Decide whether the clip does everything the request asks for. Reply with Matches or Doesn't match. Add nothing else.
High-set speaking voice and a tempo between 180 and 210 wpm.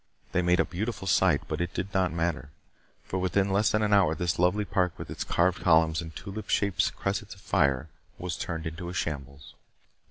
Doesn't match